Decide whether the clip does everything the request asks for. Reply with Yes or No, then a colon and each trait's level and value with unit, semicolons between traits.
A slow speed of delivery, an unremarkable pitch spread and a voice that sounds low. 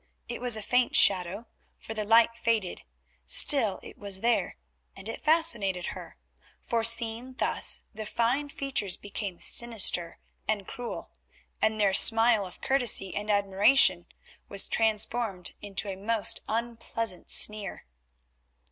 No: slow, 130 wpm; average, 3.0 semitones; high, 220 Hz